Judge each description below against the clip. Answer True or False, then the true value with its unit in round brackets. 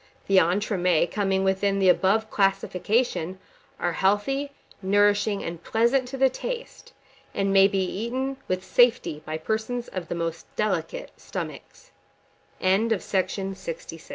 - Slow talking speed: True (120 wpm)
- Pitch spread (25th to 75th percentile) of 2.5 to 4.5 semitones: True (3.4 semitones)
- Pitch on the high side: True (195 Hz)